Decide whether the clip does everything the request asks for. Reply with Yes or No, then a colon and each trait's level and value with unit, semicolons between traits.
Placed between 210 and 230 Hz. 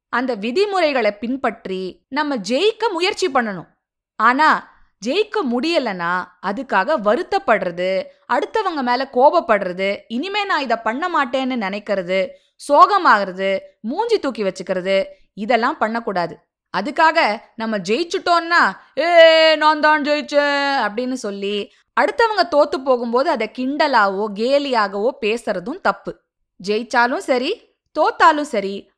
No: very high, 255 Hz